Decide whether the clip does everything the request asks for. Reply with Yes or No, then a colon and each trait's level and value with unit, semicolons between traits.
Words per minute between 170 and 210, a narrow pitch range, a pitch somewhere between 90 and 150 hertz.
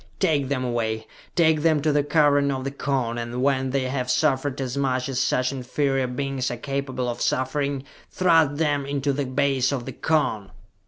Yes: average, 190 wpm; narrow, 2.0 semitones; low, 135 Hz